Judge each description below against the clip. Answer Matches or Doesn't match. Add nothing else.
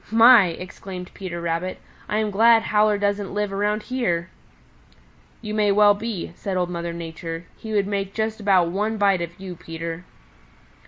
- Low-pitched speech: Doesn't match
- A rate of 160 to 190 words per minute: Matches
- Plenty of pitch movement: Doesn't match